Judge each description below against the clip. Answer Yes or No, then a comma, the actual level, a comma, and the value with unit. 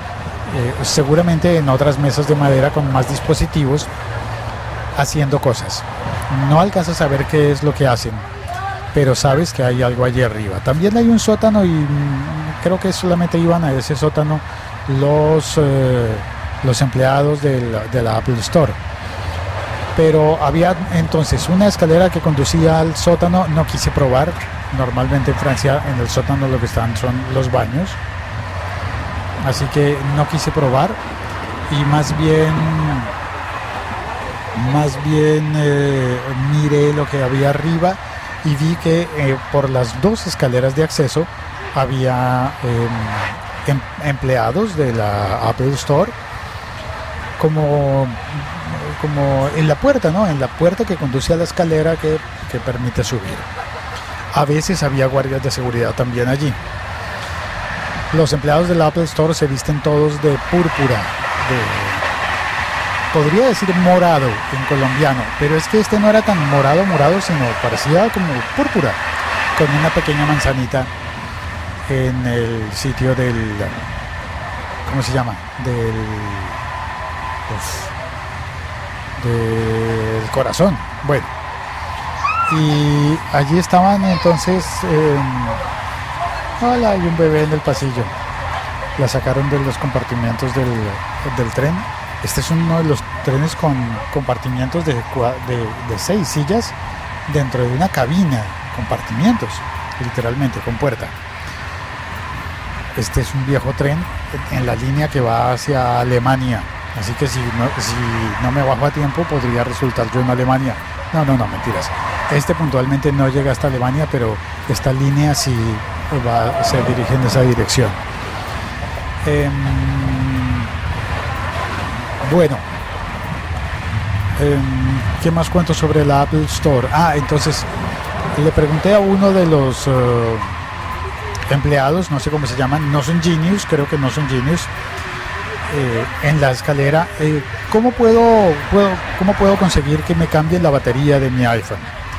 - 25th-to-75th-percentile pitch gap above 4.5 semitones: Yes, average, 5.3 semitones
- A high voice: No, low, 130 Hz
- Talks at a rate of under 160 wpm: Yes, average, 135 wpm